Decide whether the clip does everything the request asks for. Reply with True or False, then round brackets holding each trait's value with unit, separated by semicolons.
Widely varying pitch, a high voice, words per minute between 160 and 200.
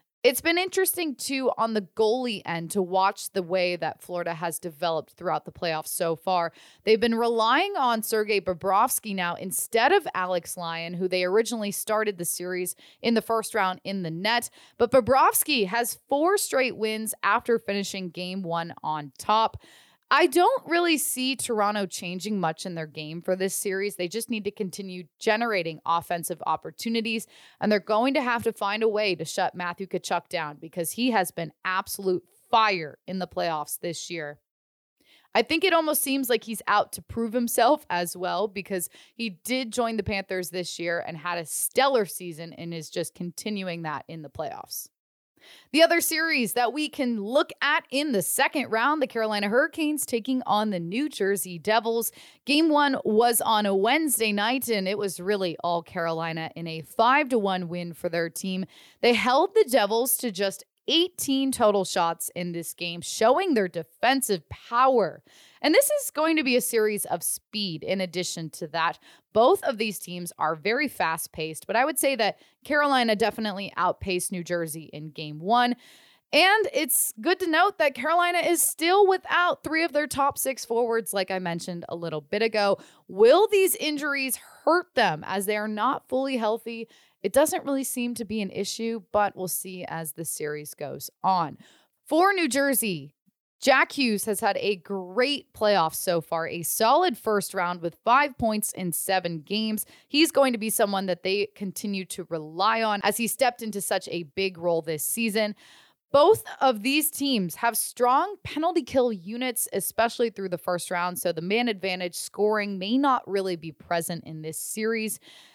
True (6.3 semitones; 210 Hz; 180 wpm)